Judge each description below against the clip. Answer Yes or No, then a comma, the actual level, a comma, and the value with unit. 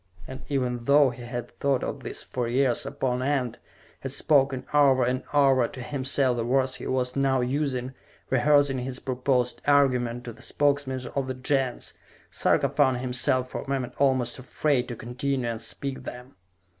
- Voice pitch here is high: No, low, 130 Hz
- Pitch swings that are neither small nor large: No, narrow, 1.8 semitones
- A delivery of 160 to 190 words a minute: Yes, average, 170 wpm